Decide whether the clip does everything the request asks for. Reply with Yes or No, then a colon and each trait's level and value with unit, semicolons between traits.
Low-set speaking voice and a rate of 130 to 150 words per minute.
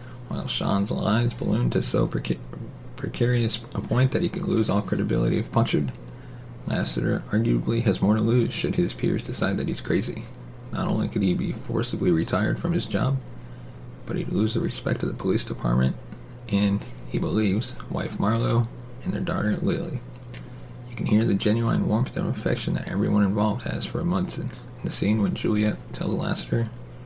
No: low, 105 Hz; average, 180 wpm